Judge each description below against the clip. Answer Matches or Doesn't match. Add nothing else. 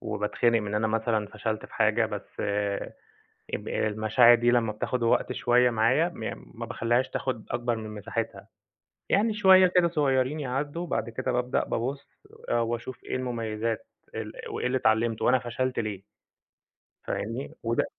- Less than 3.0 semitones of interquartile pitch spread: Matches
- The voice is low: Matches